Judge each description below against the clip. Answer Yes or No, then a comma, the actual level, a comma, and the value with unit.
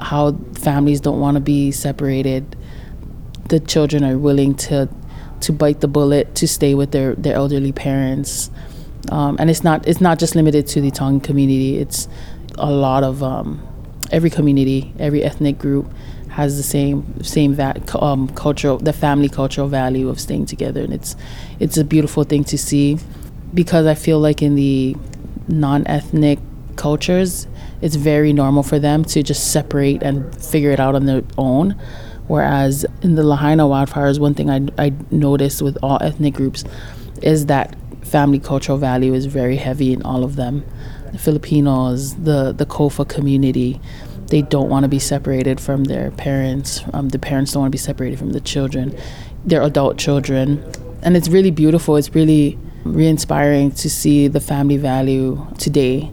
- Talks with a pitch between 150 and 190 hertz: No, medium, 140 Hz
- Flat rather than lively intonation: Yes, narrow, 1.7 semitones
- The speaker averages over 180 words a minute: No, average, 170 wpm